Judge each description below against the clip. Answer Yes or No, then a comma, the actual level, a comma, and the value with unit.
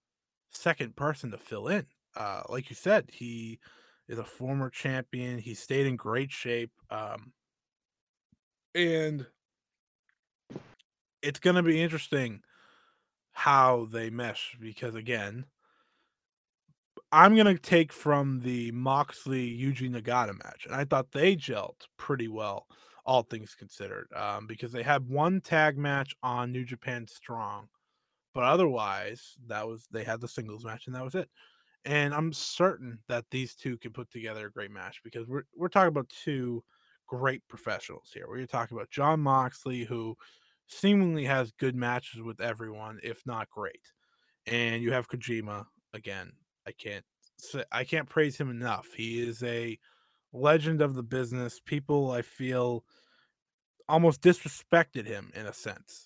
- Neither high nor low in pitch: No, low, 125 Hz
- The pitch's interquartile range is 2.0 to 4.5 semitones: Yes, average, 3.8 semitones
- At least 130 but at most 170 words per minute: Yes, average, 150 wpm